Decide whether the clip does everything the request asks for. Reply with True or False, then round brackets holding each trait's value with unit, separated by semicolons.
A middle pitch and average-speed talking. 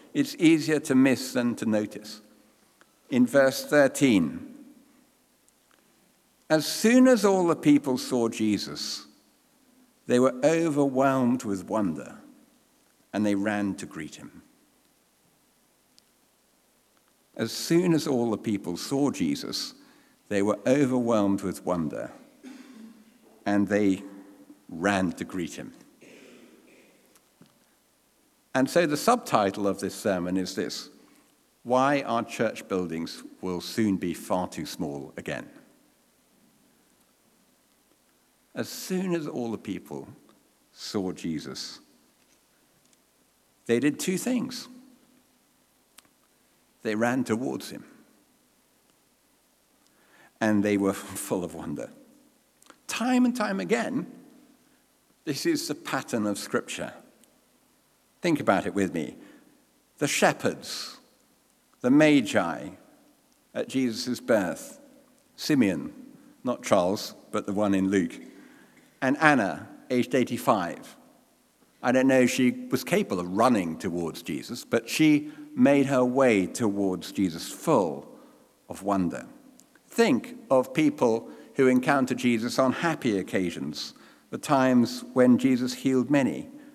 False (145 Hz; 110 wpm)